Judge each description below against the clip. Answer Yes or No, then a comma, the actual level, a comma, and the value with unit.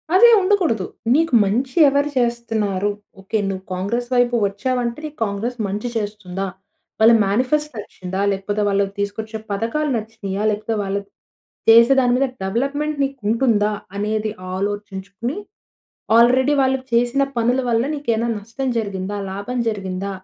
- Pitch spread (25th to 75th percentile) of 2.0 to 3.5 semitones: No, average, 4.0 semitones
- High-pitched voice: Yes, high, 225 Hz